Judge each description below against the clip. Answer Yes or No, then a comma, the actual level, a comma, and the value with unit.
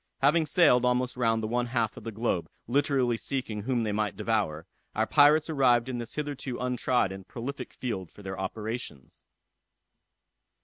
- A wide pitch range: No, average, 3.3 semitones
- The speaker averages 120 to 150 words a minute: No, average, 165 wpm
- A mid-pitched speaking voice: No, low, 120 Hz